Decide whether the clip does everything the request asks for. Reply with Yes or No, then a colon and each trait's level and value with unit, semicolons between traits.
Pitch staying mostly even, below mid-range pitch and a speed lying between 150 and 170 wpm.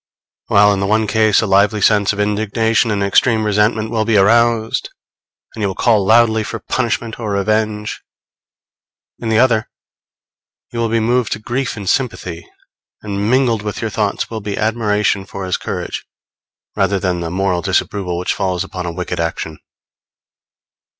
Yes: narrow, 2.2 semitones; low, 105 Hz; average, 165 wpm